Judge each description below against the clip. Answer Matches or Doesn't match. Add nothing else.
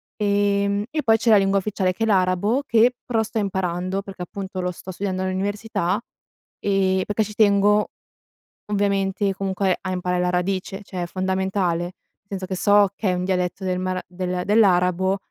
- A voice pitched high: Matches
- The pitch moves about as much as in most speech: Doesn't match